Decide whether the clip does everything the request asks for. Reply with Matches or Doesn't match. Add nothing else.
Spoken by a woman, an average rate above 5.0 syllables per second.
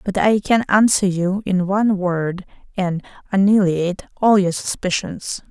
Doesn't match